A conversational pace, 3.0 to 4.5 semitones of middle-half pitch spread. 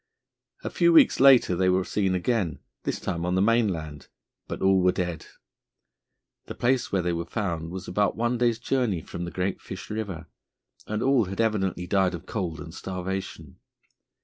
Yes: average, 175 wpm; average, 4.2 semitones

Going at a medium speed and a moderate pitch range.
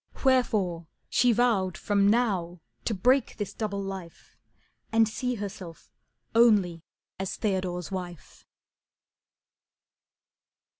No: slow, 95 wpm; average, 4.0 semitones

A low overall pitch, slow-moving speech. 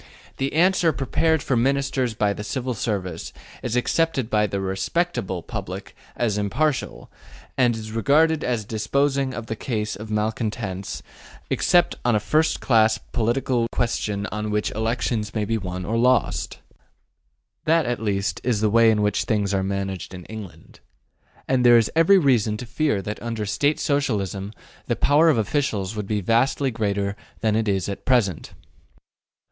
No: low, 110 Hz; average, 160 wpm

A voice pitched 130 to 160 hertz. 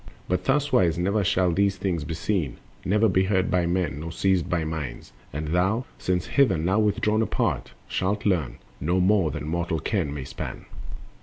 No: very low, 90 Hz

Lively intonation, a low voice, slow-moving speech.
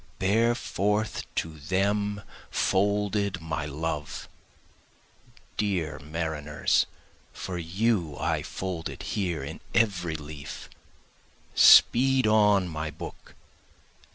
No: average, 4.7 semitones; very low, 95 Hz; slow, 95 wpm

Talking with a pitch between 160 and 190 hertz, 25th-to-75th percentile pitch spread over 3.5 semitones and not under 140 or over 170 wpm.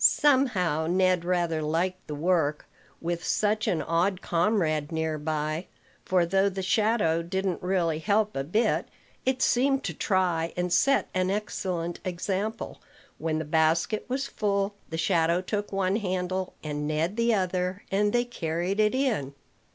Yes: medium, 185 Hz; average, 3.9 semitones; average, 150 wpm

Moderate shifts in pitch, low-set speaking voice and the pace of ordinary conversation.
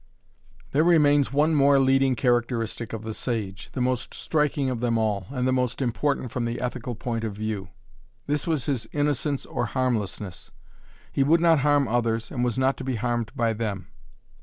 Yes: average, 3.5 semitones; low, 125 Hz; average, 185 wpm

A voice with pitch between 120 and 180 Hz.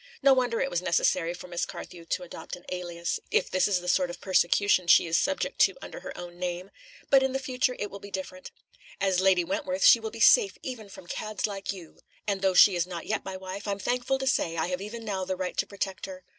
No: high, 190 Hz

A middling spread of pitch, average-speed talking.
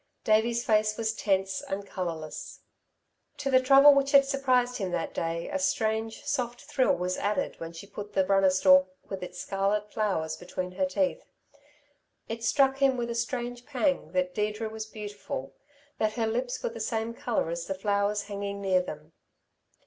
Yes: average, 4.3 semitones; average, 175 wpm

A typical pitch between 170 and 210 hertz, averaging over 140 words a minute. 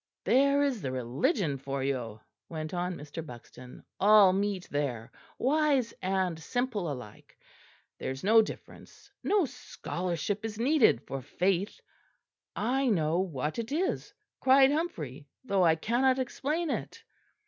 No: high, 190 Hz; slow, 135 wpm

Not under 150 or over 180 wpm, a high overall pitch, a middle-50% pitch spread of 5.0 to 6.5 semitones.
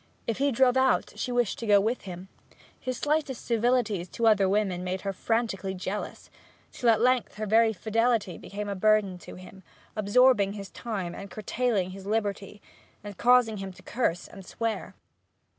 No: average, 175 wpm; high, 215 Hz; average, 3.5 semitones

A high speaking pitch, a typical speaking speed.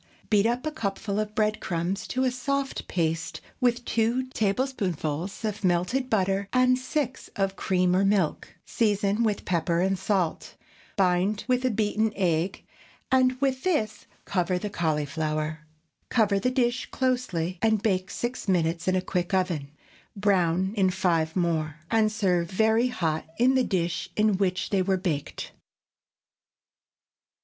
Yes: high, 195 Hz; average, 145 wpm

